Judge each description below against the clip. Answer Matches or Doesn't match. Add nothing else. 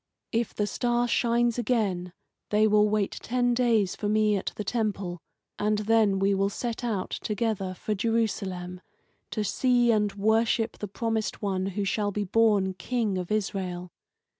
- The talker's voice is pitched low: Doesn't match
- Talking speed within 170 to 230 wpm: Doesn't match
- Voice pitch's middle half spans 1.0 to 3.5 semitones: Matches